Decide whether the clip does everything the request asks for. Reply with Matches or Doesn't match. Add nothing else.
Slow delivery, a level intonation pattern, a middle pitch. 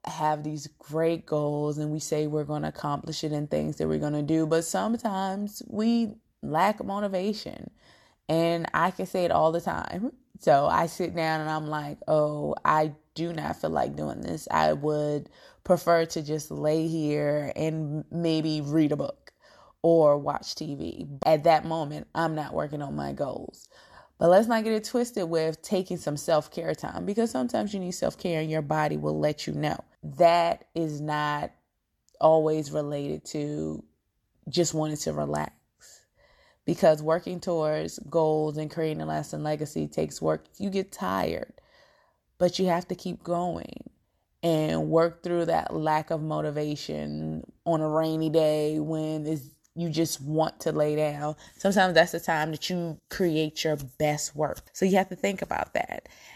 Doesn't match